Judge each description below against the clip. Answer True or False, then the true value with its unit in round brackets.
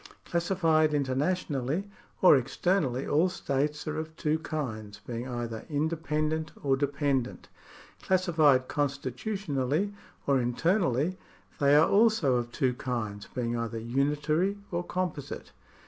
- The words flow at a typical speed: False (115 wpm)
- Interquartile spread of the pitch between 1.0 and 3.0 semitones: False (4.3 semitones)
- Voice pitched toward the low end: False (145 Hz)